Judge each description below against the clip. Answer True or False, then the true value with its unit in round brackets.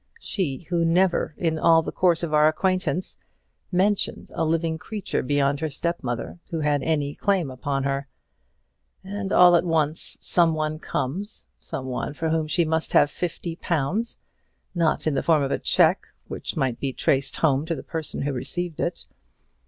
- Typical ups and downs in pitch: True (3.4 semitones)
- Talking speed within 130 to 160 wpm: False (175 wpm)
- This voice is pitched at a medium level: True (160 Hz)